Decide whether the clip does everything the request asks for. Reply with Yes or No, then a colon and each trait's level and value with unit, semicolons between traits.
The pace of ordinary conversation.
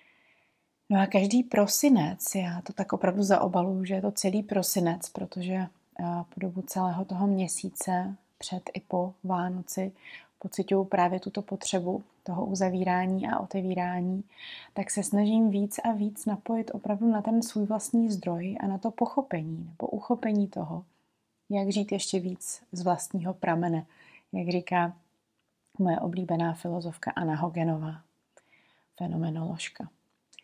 Yes: average, 130 wpm